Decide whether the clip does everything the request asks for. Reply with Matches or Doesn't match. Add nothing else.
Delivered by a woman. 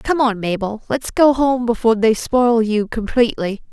Matches